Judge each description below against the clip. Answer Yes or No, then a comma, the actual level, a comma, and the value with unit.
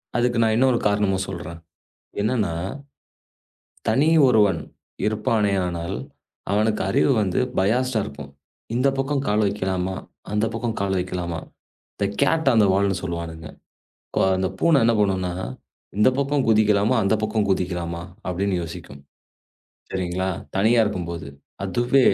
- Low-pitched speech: Yes, low, 100 Hz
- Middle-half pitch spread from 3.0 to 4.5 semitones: Yes, average, 3.9 semitones